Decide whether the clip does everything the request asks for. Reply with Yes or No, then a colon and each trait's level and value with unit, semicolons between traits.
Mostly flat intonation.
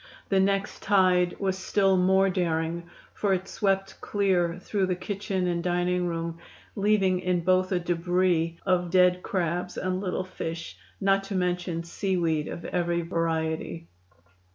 Yes: narrow, 1.9 semitones